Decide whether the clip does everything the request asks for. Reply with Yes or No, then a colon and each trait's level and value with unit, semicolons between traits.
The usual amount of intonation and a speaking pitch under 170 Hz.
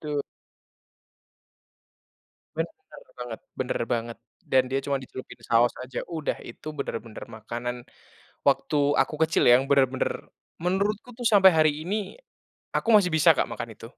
No: wide, 6.6 semitones; medium, 140 Hz